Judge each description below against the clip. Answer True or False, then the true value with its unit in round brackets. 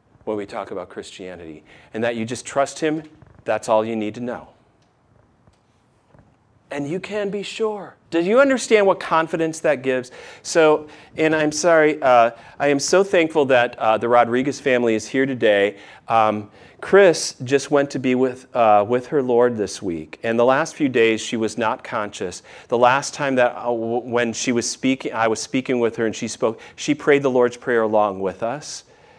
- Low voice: True (125 Hz)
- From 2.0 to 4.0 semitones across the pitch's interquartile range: False (4.9 semitones)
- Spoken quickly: False (190 wpm)